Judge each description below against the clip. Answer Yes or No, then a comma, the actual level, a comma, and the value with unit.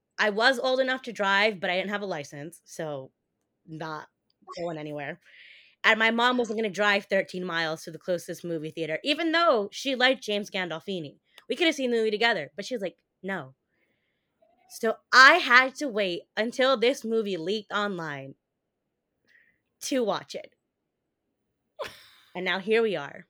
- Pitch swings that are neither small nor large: No, wide, 6.1 semitones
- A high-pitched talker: Yes, high, 205 Hz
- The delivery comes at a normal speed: Yes, average, 170 wpm